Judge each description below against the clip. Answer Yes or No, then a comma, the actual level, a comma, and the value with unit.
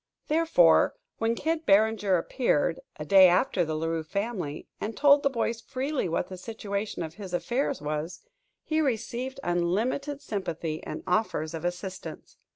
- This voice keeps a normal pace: Yes, average, 155 wpm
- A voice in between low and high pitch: No, high, 200 Hz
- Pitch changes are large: Yes, wide, 6.3 semitones